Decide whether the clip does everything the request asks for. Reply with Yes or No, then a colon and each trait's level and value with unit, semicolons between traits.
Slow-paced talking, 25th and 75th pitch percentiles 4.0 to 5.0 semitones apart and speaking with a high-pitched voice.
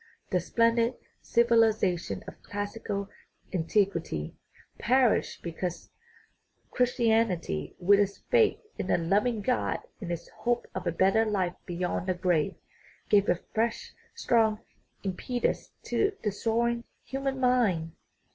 Yes: slow, 120 wpm; average, 4.6 semitones; high, 205 Hz